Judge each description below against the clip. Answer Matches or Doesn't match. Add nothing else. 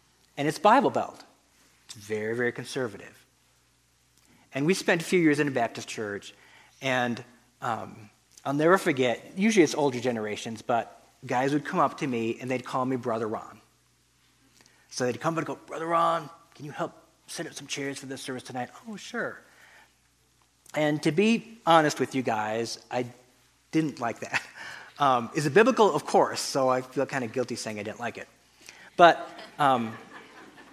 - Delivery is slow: Doesn't match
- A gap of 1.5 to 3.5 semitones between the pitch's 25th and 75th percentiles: Doesn't match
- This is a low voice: Matches